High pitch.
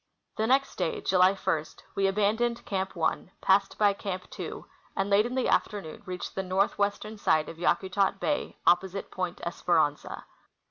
Yes: high, 195 Hz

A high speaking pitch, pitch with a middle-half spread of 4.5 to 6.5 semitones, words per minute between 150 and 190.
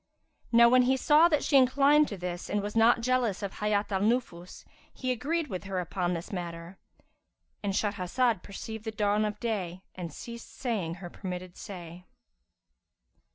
Yes: high, 210 Hz; average, 4.9 semitones; average, 165 wpm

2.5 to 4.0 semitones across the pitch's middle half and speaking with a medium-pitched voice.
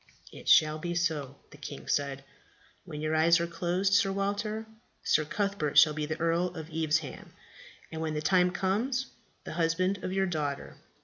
Yes: average, 3.6 semitones; medium, 165 Hz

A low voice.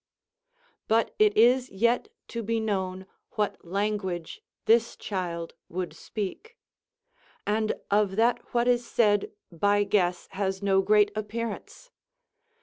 No: high, 210 Hz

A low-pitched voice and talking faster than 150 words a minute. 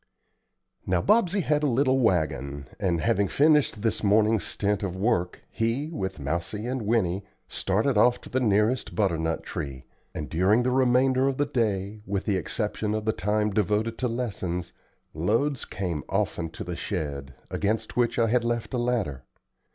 Yes: low, 105 Hz; average, 165 wpm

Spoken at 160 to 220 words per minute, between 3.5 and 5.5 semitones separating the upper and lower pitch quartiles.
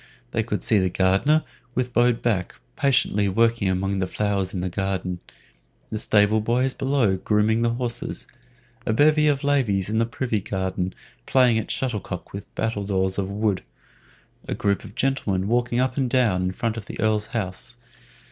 Yes: average, 170 wpm; average, 4.0 semitones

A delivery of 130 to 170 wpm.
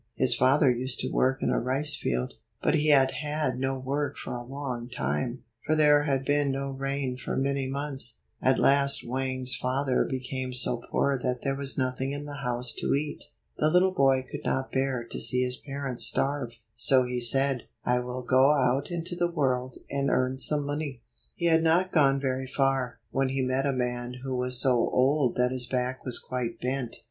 No: average, 200 wpm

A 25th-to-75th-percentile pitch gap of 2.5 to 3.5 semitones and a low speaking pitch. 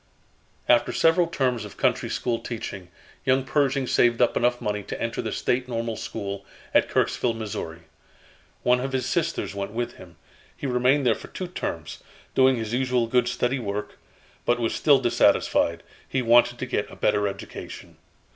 Yes: average, 2.8 semitones; low, 120 Hz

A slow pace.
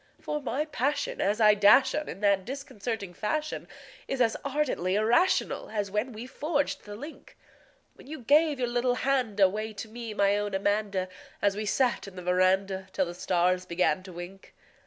No: average, 180 wpm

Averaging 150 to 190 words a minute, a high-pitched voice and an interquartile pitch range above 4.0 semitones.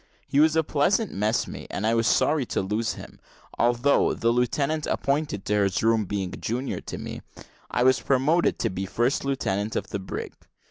No: average, 185 wpm; low, 120 Hz; average, 5.0 semitones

